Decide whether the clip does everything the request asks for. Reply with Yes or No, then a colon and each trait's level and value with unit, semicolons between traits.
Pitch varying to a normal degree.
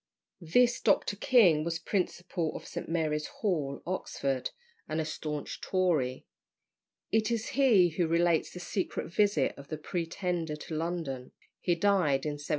Yes: average, 3.6 semitones